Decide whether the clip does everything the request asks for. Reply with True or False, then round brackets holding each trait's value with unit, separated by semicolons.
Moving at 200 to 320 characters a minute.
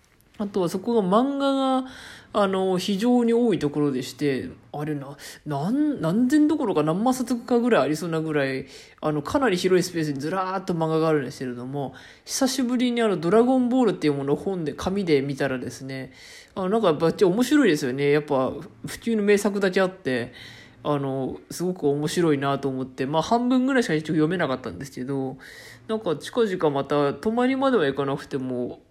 False (395 characters per minute)